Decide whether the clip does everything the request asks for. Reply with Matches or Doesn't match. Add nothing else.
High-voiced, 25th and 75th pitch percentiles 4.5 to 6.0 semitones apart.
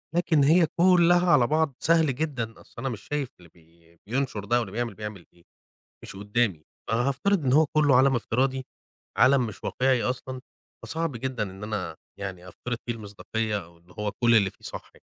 Doesn't match